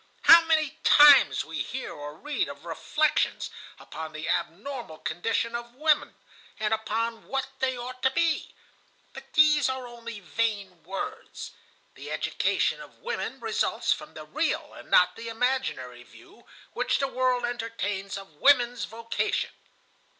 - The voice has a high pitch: Yes, high, 235 Hz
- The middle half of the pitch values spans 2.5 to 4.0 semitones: No, average, 5.2 semitones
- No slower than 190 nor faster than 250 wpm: No, average, 140 wpm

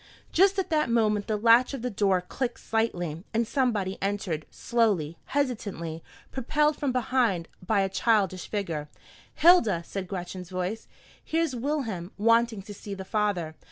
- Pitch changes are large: No, average, 4.9 semitones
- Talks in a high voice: Yes, high, 210 Hz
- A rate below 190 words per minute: Yes, average, 150 wpm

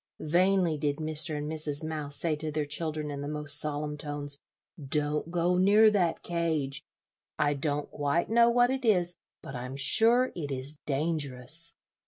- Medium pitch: Yes, medium, 155 Hz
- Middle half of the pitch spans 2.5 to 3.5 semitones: Yes, average, 2.9 semitones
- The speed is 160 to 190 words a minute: Yes, average, 165 wpm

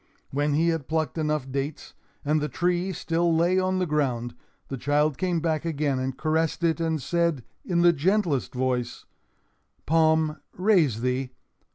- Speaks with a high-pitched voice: No, medium, 155 Hz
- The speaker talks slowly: No, average, 160 wpm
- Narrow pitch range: No, average, 3.5 semitones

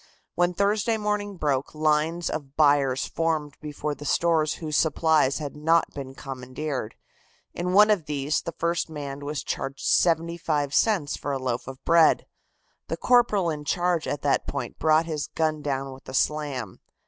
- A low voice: No, medium, 155 Hz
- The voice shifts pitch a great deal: No, average, 3.0 semitones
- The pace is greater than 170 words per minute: No, average, 165 wpm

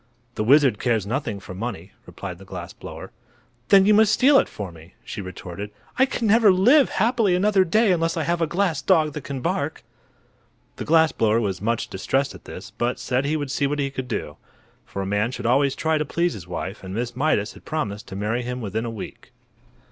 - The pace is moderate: No, fast, 220 wpm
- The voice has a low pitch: Yes, low, 130 Hz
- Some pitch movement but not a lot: No, wide, 8.3 semitones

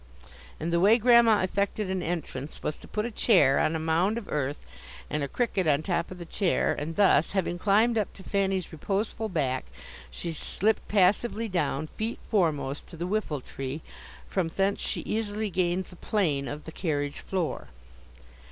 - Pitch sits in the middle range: Yes, medium, 180 Hz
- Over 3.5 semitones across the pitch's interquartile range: Yes, average, 4.9 semitones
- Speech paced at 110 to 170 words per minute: No, average, 180 wpm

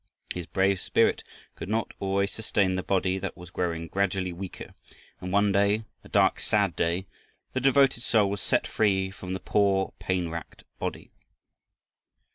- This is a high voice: No, very low, 95 Hz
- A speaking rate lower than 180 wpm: Yes, average, 160 wpm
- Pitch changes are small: Yes, narrow, 1.7 semitones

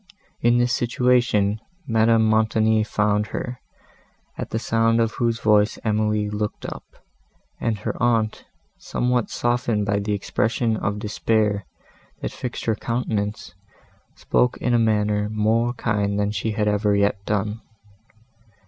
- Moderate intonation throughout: No, narrow, 1.9 semitones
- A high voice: No, low, 110 Hz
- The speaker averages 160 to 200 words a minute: No, slow, 135 wpm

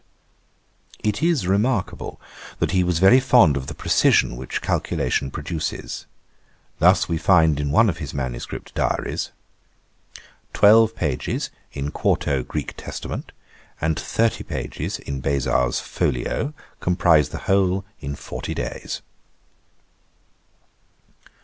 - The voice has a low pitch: Yes, very low, 80 Hz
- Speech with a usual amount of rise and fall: No, wide, 6.1 semitones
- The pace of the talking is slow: Yes, slow, 115 wpm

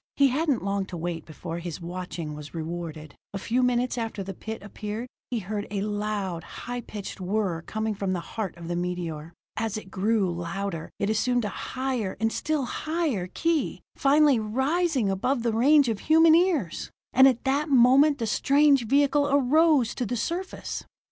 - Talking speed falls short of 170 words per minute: No, average, 175 wpm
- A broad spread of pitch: Yes, wide, 6.5 semitones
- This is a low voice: No, high, 220 Hz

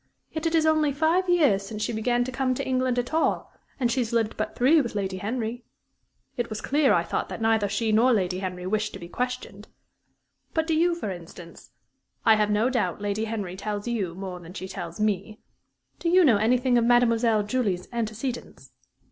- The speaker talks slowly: No, fast, 205 wpm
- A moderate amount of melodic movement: Yes, average, 4.0 semitones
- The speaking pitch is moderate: No, high, 225 Hz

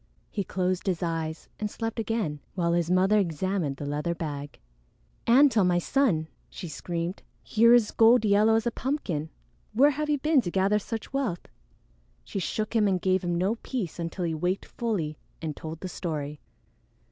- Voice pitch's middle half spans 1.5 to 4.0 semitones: No, average, 5.1 semitones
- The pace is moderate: Yes, average, 175 wpm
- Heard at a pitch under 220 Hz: Yes, medium, 185 Hz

